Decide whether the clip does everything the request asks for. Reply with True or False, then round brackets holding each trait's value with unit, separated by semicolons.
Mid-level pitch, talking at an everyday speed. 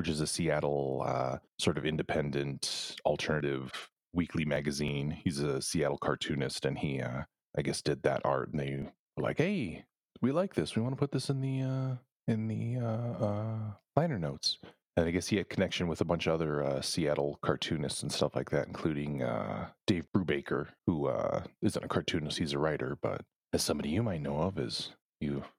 False (80 Hz; 195 wpm)